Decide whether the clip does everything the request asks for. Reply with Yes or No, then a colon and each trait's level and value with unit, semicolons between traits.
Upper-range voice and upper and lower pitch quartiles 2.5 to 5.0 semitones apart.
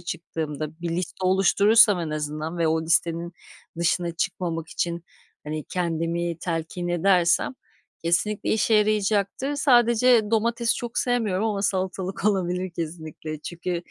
No: medium, 175 Hz; average, 4.0 semitones